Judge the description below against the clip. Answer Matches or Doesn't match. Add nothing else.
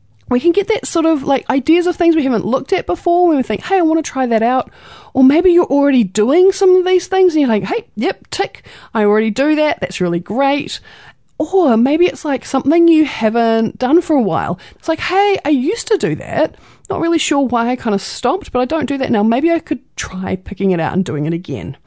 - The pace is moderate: Doesn't match